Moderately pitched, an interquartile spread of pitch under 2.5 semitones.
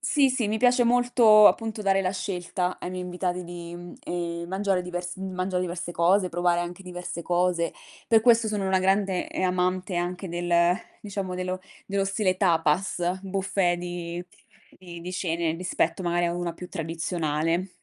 Yes: medium, 180 Hz; narrow, 1.9 semitones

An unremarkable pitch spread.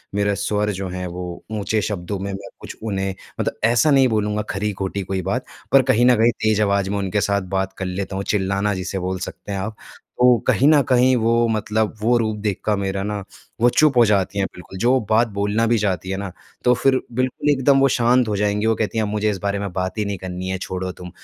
Yes: average, 3.1 semitones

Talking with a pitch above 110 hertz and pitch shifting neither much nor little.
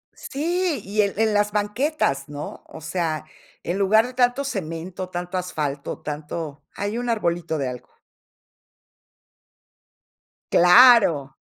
No: medium, 185 Hz; wide, 6.3 semitones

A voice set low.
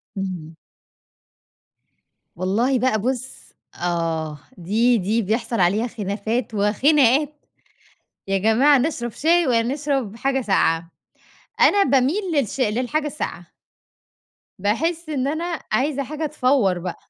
No: high, 240 Hz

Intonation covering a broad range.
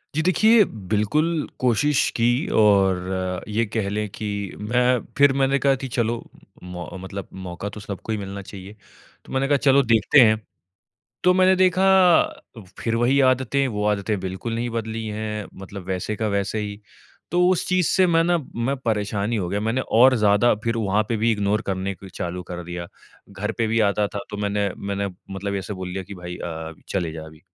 No: average, 4.4 semitones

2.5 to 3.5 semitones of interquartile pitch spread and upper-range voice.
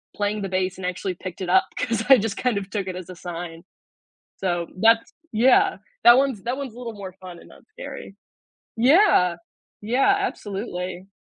No: average, 5.0 semitones; high, 200 Hz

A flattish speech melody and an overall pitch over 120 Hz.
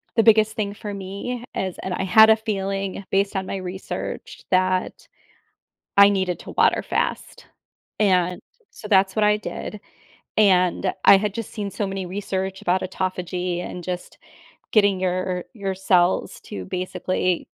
Yes: narrow, 1.8 semitones; high, 190 Hz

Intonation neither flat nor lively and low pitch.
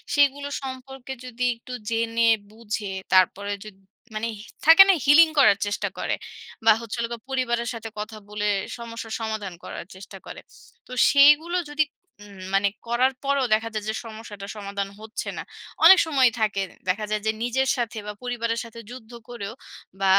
No: average, 3.6 semitones; high, 230 Hz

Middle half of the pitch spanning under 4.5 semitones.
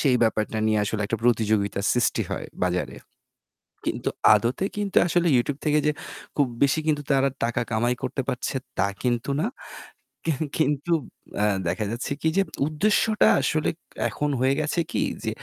No: wide, 5.4 semitones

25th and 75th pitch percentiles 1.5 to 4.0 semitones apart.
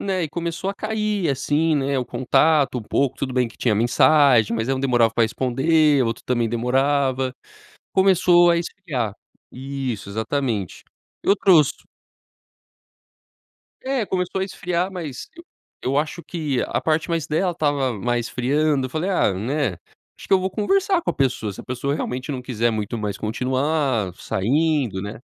No: wide, 5.4 semitones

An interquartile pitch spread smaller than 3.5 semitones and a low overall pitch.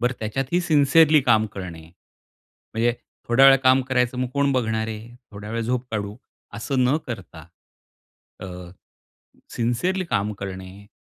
No: average, 4.1 semitones; low, 120 Hz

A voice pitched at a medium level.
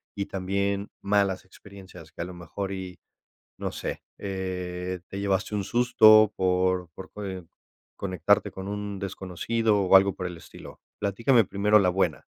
No: very low, 95 Hz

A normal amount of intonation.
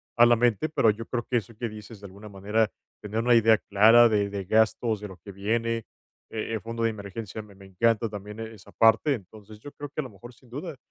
No: narrow, 2.2 semitones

